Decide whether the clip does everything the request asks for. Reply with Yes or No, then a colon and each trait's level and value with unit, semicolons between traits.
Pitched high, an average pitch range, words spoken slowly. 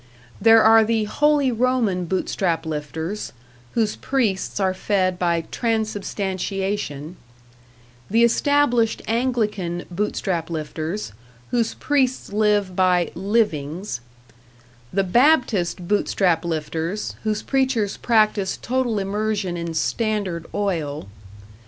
Yes: high, 205 Hz; average, 4.4 semitones; slow, 95 wpm